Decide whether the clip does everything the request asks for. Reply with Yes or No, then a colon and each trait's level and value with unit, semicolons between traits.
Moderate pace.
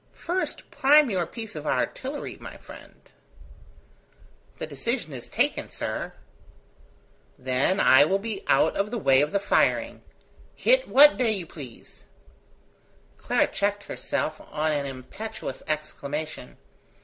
No: slow, 125 wpm